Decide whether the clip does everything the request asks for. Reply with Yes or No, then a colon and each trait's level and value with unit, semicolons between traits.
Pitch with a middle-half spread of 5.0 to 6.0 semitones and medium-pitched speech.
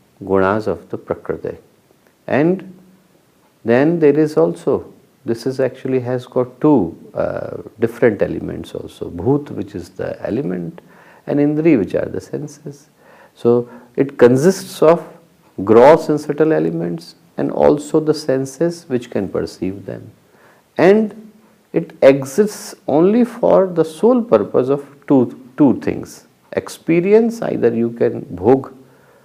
Yes: average, 5.3 semitones; medium, 145 Hz